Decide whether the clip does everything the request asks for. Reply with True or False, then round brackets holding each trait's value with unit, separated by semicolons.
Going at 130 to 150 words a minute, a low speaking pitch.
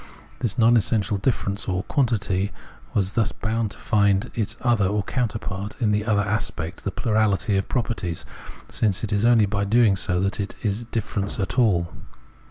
False (170 wpm; 105 Hz)